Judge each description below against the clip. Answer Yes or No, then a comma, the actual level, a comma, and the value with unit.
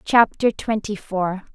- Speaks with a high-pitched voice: Yes, high, 205 Hz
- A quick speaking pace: No, slow, 115 wpm